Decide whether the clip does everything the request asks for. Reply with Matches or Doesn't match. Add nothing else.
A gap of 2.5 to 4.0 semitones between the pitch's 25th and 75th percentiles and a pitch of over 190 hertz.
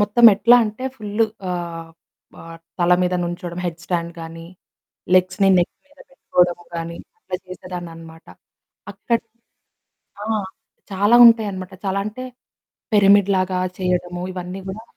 Doesn't match